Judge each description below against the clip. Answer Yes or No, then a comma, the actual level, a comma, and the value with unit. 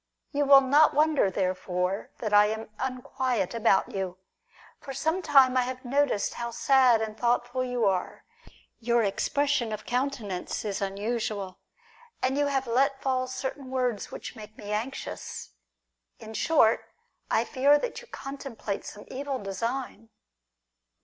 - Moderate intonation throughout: Yes, average, 4.4 semitones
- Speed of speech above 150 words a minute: No, average, 145 wpm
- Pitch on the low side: No, high, 245 Hz